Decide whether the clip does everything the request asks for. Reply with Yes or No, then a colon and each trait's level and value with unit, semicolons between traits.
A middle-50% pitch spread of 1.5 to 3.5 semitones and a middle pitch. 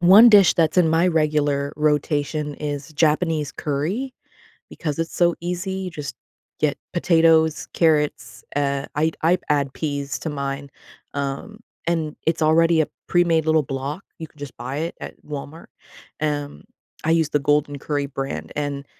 Yes: narrow, 2.4 semitones; medium, 150 Hz